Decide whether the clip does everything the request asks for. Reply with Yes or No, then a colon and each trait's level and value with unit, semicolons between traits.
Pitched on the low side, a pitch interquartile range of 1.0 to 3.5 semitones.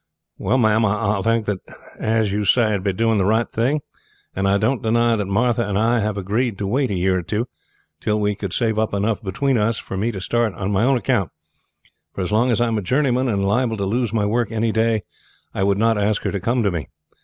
Yes: low, 110 Hz; average, 2.8 semitones